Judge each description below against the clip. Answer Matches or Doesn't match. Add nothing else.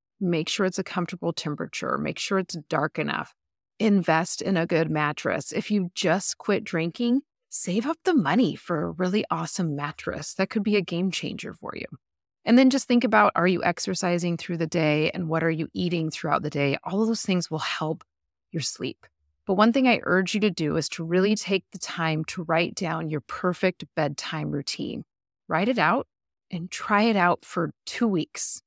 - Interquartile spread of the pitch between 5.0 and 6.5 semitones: Doesn't match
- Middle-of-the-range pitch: Matches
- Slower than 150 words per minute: Doesn't match